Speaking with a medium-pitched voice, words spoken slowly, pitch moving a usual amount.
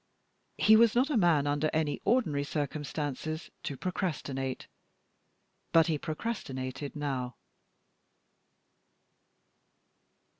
Yes: medium, 150 Hz; slow, 85 wpm; average, 3.8 semitones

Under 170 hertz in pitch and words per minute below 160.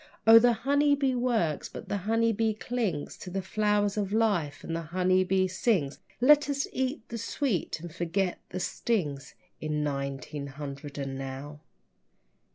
No: high, 190 Hz; average, 150 wpm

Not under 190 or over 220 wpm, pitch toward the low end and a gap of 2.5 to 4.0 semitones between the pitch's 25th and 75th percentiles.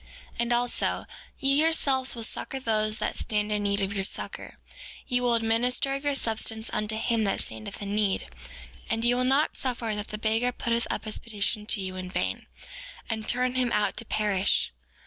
No: average, 195 wpm; high, 225 Hz; average, 2.8 semitones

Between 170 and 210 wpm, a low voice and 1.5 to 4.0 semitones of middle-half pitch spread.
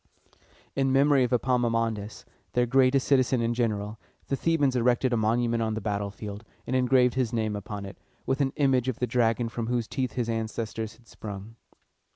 Yes: average, 180 wpm; low, 120 Hz; narrow, 2.6 semitones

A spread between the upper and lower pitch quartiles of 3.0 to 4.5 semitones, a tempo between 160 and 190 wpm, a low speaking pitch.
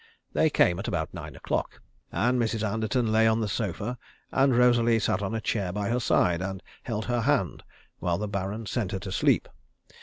No: average, 3.4 semitones; average, 200 wpm; low, 110 Hz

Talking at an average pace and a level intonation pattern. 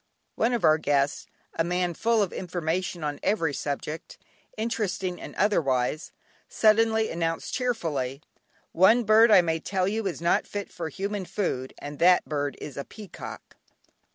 No: average, 155 wpm; average, 5.2 semitones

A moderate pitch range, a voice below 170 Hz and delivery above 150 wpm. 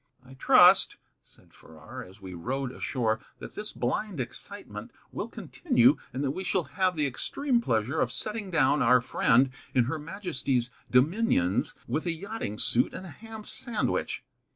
No: wide, 7.3 semitones; medium, 140 Hz; average, 160 wpm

